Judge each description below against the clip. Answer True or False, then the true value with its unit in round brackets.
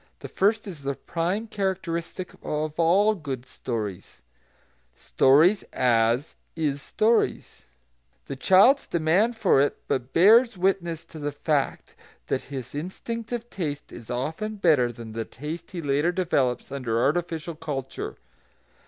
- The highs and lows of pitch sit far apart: True (5.8 semitones)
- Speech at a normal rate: False (130 wpm)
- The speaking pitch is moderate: True (160 Hz)